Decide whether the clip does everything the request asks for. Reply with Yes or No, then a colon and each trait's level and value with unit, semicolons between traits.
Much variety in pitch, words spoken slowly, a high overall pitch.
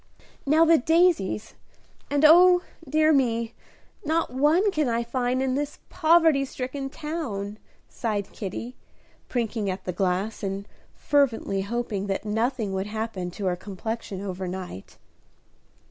Yes: wide, 6.7 semitones; slow, 130 wpm; high, 235 Hz